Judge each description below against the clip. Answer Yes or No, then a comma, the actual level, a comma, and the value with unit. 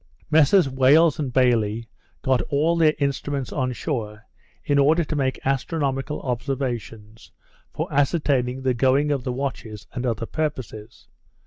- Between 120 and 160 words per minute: Yes, slow, 135 wpm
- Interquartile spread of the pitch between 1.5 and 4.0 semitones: Yes, average, 2.9 semitones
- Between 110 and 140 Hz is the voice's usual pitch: Yes, low, 135 Hz